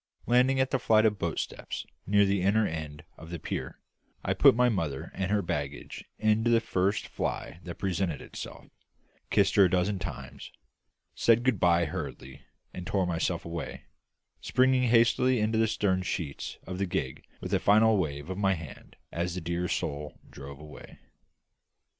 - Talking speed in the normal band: Yes, average, 170 wpm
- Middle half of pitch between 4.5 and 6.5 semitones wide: Yes, average, 4.8 semitones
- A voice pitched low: Yes, very low, 95 Hz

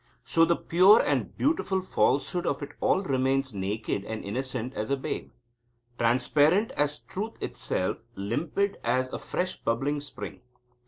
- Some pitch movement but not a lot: No, wide, 6.9 semitones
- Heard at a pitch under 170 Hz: Yes, medium, 140 Hz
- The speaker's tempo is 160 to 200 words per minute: No, average, 140 wpm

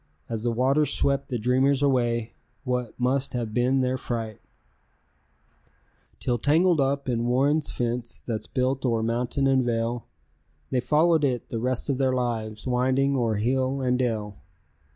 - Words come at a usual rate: Yes, average, 150 wpm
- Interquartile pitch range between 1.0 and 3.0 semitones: Yes, narrow, 2.4 semitones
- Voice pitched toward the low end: Yes, low, 125 Hz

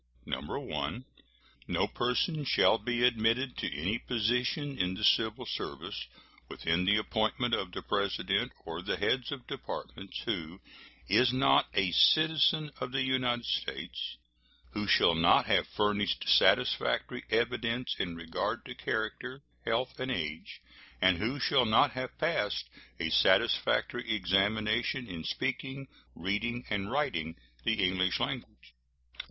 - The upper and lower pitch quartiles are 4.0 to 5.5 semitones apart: Yes, average, 5.2 semitones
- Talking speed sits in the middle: No, slow, 130 wpm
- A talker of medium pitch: No, low, 110 Hz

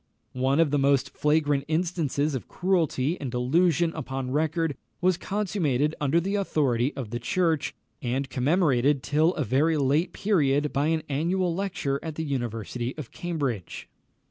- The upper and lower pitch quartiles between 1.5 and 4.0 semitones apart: Yes, average, 3.7 semitones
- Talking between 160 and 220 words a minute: No, average, 150 wpm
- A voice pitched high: No, medium, 150 Hz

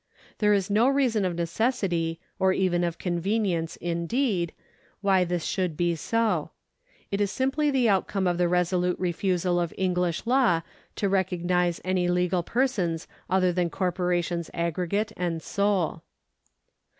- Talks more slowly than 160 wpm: Yes, average, 140 wpm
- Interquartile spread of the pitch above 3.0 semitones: No, average, 2.7 semitones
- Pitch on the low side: No, medium, 180 Hz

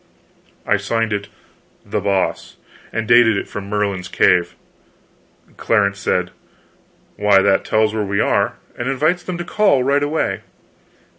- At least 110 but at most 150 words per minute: Yes, average, 140 wpm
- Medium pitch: No, low, 105 Hz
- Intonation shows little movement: No, average, 4.3 semitones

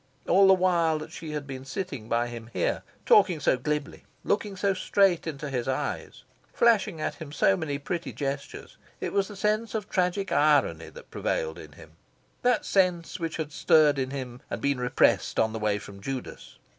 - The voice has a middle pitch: Yes, medium, 155 Hz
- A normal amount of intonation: No, wide, 6.0 semitones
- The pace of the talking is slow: No, average, 190 wpm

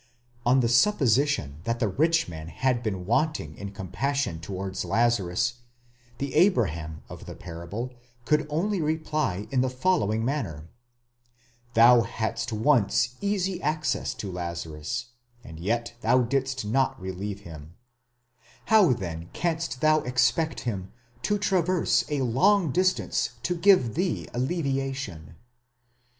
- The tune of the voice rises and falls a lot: Yes, wide, 8.0 semitones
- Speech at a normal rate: No, slow, 130 wpm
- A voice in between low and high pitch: No, low, 120 Hz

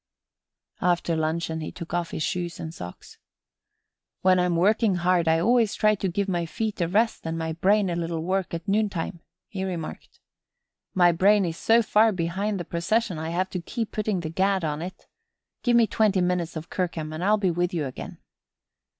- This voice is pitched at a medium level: Yes, medium, 180 Hz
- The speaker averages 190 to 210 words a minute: Yes, average, 195 wpm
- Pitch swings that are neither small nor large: Yes, average, 3.3 semitones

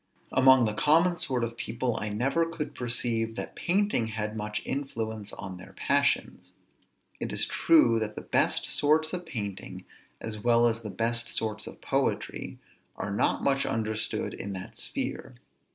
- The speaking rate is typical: Yes, average, 160 wpm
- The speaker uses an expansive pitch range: No, average, 4.2 semitones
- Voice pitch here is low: Yes, low, 115 Hz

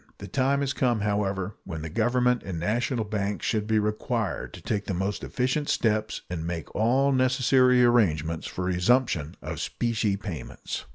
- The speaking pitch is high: No, low, 110 Hz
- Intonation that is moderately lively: Yes, average, 4.5 semitones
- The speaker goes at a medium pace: Yes, average, 170 wpm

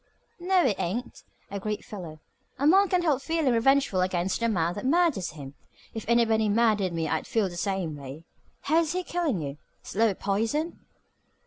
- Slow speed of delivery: No, average, 165 wpm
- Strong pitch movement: Yes, wide, 7.7 semitones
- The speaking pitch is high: Yes, high, 220 Hz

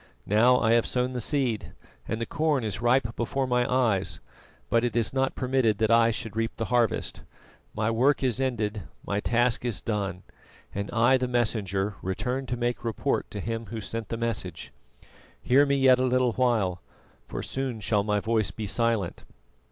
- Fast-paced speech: No, average, 185 wpm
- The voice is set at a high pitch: No, low, 115 Hz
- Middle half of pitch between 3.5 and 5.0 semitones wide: No, average, 2.8 semitones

